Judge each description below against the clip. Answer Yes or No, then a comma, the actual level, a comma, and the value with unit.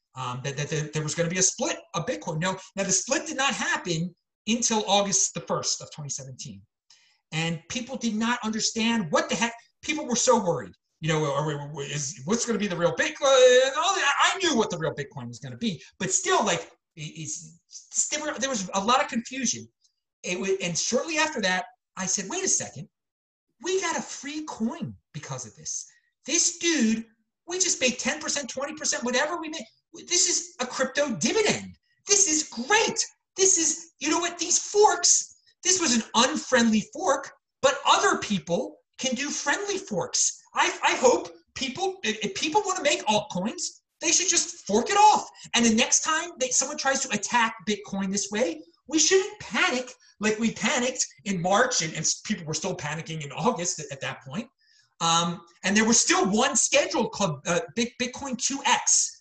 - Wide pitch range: Yes, wide, 9.0 semitones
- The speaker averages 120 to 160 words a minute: No, average, 185 wpm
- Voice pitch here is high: Yes, high, 235 Hz